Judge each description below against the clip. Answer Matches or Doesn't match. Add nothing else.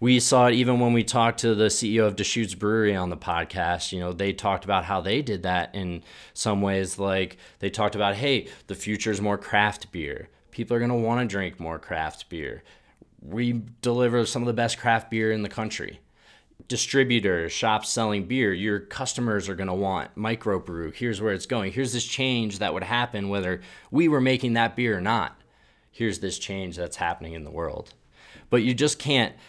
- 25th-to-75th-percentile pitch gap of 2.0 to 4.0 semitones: Matches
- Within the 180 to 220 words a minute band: Matches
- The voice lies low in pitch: Matches